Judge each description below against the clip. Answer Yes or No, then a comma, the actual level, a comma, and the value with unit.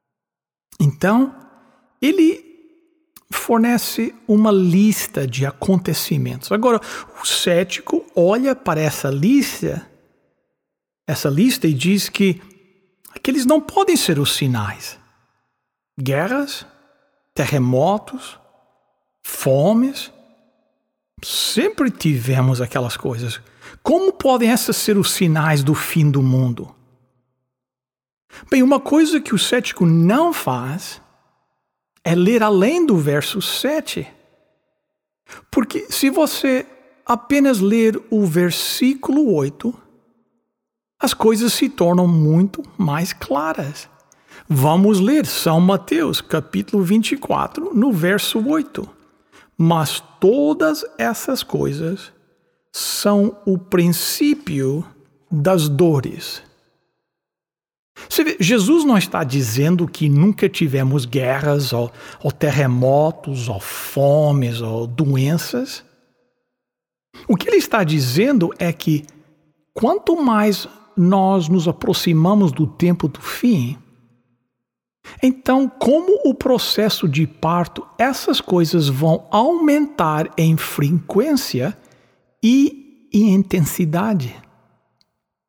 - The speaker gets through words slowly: Yes, slow, 95 wpm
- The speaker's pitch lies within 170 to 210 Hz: Yes, high, 190 Hz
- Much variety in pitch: Yes, wide, 9.0 semitones